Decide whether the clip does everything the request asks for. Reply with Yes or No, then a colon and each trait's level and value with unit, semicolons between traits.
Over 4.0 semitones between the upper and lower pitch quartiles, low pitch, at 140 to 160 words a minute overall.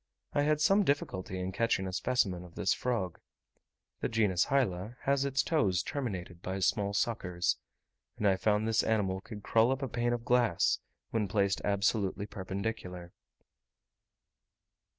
Yes: average, 4.4 semitones; low, 105 Hz; average, 150 wpm